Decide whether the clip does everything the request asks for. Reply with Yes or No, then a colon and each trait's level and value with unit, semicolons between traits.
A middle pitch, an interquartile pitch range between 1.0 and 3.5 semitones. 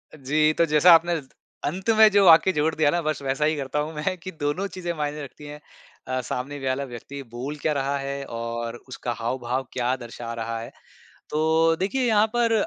No: medium, 150 Hz; average, 4.0 semitones